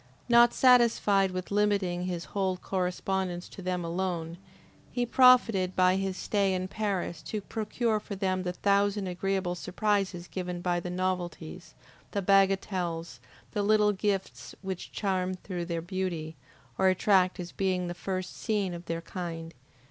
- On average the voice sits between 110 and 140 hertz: No, medium, 185 Hz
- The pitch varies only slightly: Yes, narrow, 2.2 semitones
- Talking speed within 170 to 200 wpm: No, average, 150 wpm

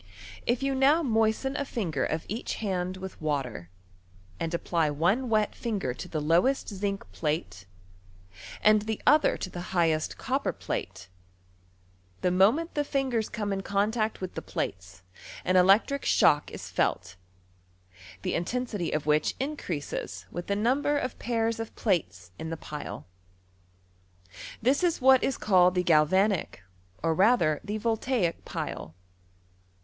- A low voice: No, high, 195 Hz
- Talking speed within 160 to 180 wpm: No, average, 145 wpm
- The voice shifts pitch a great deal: Yes, wide, 6.4 semitones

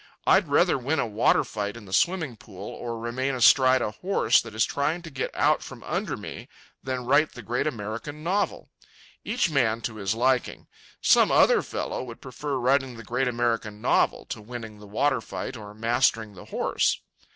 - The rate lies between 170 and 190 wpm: Yes, average, 185 wpm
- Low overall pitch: Yes, low, 120 Hz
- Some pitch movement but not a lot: Yes, average, 3.6 semitones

